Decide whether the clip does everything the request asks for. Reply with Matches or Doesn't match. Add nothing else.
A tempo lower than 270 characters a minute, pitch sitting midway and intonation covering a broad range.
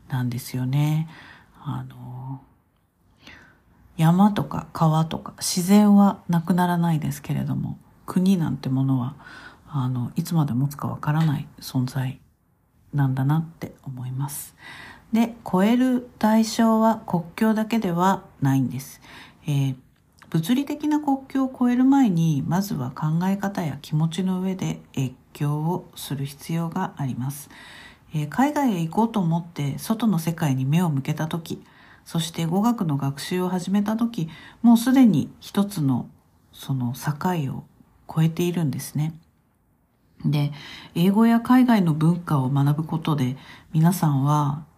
Matches